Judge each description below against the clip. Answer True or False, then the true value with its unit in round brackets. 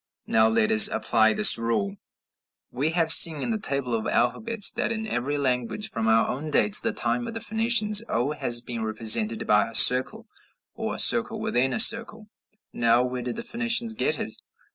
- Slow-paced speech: False (195 wpm)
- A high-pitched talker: False (130 Hz)